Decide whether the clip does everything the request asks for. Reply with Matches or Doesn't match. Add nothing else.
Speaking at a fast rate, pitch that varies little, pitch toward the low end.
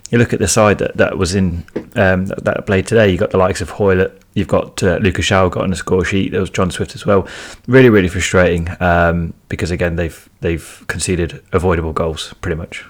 Matches